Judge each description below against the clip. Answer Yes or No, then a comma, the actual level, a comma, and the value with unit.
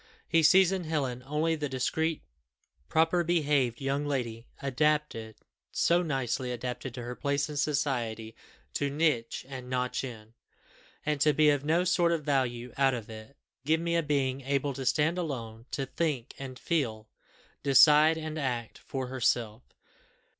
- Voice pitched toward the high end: No, medium, 140 Hz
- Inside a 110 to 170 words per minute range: Yes, average, 155 wpm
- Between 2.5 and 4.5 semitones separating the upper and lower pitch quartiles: Yes, average, 3.8 semitones